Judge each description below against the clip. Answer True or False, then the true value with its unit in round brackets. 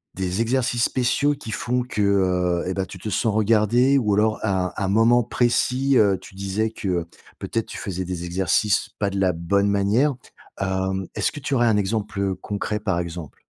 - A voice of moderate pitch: False (100 Hz)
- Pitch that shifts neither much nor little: True (3.5 semitones)